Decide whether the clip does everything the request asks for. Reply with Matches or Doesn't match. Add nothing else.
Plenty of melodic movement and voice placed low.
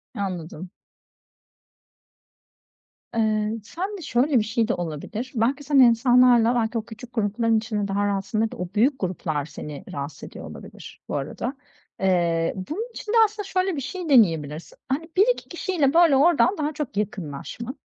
Doesn't match